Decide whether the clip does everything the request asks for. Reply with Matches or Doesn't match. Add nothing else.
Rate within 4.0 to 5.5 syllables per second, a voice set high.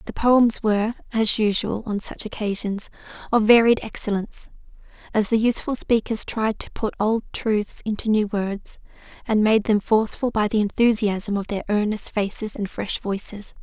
Matches